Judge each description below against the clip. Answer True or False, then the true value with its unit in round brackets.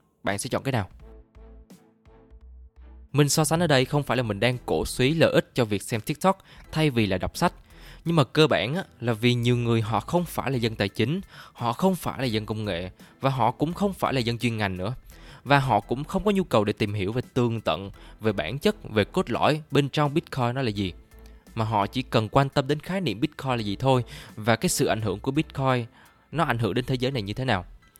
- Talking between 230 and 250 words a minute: True (245 wpm)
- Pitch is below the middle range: True (125 Hz)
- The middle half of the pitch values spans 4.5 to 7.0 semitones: True (5.2 semitones)